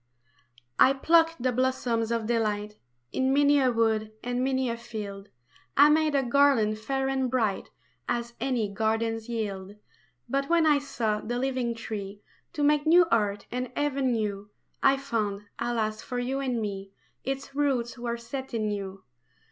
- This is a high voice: Yes, high, 240 Hz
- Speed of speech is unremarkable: Yes, average, 160 wpm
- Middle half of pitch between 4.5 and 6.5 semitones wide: No, average, 3.8 semitones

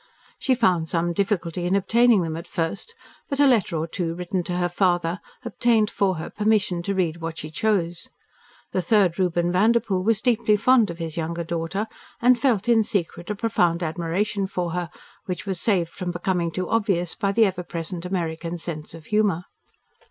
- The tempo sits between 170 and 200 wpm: Yes, average, 185 wpm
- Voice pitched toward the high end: No, medium, 180 Hz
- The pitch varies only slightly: No, average, 3.7 semitones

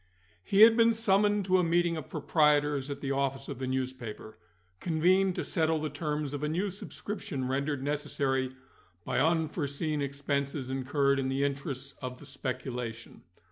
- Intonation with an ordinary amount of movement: Yes, average, 3.6 semitones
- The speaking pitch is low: No, medium, 145 Hz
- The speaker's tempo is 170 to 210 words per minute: No, average, 160 wpm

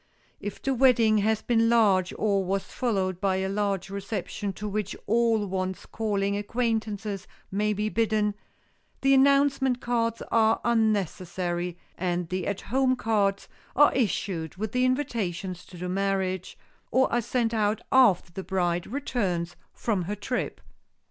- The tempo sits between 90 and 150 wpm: Yes, average, 145 wpm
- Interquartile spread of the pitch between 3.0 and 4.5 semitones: Yes, average, 3.5 semitones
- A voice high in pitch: Yes, high, 210 Hz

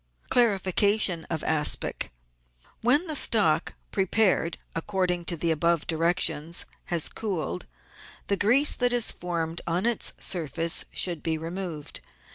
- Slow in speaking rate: Yes, slow, 125 wpm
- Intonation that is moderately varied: Yes, average, 3.9 semitones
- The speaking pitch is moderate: Yes, medium, 175 Hz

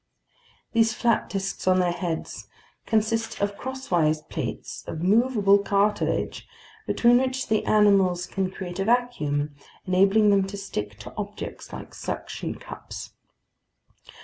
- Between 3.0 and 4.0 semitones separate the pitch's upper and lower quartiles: Yes, average, 3.5 semitones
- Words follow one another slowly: Yes, slow, 125 wpm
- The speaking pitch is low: No, high, 200 Hz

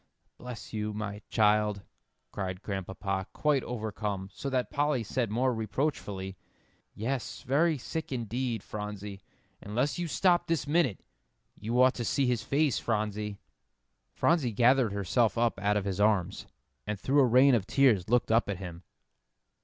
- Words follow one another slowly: No, average, 150 wpm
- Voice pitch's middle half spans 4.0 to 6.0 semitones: Yes, average, 4.3 semitones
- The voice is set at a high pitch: No, low, 110 Hz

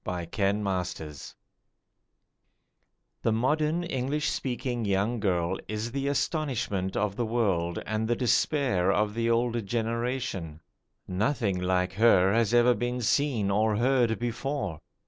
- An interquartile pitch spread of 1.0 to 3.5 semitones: No, average, 4.3 semitones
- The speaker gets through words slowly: Yes, slow, 125 wpm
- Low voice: Yes, low, 115 Hz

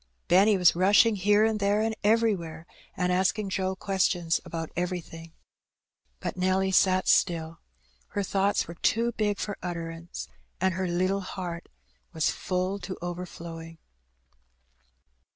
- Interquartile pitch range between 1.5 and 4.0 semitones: Yes, average, 2.7 semitones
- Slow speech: Yes, slow, 130 wpm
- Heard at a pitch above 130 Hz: Yes, medium, 185 Hz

